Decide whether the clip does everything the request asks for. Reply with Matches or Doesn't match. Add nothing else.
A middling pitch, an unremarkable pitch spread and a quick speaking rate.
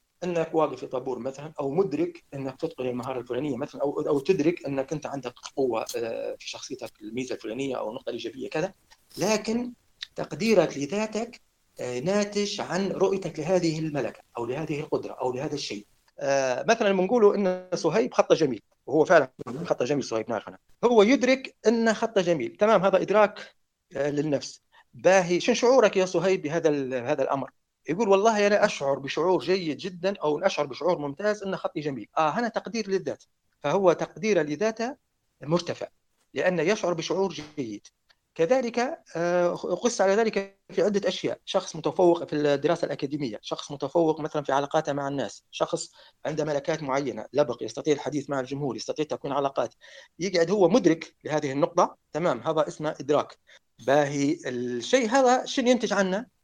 Doesn't match